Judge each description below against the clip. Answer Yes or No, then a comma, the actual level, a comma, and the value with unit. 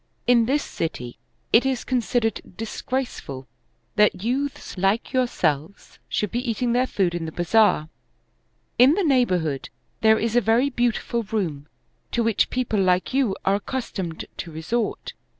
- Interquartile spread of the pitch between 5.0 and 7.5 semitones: Yes, wide, 5.4 semitones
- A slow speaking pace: No, average, 145 wpm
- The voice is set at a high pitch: Yes, high, 225 Hz